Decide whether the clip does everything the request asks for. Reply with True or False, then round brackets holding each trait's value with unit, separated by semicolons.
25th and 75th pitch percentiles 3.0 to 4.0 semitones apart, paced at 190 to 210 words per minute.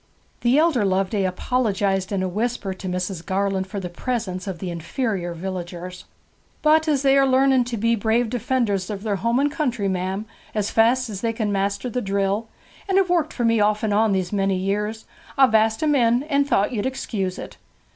False (4.4 semitones; 200 wpm)